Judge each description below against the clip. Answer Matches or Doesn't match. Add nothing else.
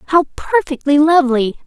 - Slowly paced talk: Matches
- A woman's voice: Matches